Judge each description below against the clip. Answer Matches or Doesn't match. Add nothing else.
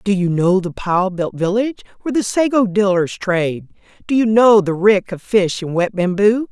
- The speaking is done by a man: Doesn't match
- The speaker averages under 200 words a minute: Doesn't match